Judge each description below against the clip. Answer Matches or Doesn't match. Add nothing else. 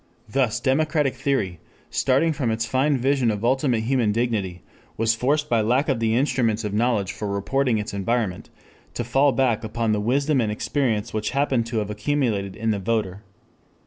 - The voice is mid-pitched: Doesn't match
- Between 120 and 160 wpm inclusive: Doesn't match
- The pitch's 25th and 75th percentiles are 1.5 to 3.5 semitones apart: Doesn't match